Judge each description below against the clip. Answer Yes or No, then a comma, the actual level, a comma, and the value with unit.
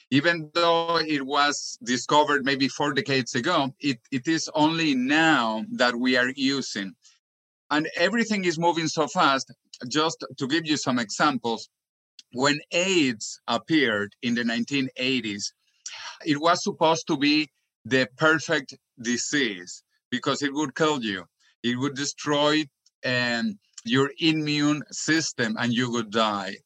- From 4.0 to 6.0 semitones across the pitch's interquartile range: Yes, average, 4.5 semitones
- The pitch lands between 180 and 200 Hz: No, medium, 140 Hz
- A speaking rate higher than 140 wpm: No, slow, 135 wpm